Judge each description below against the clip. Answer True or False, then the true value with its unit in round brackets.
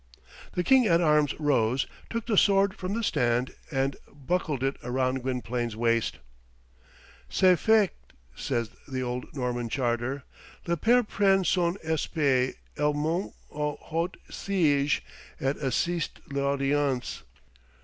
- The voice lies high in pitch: False (145 Hz)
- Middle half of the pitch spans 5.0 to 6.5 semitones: True (5.5 semitones)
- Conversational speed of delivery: False (130 wpm)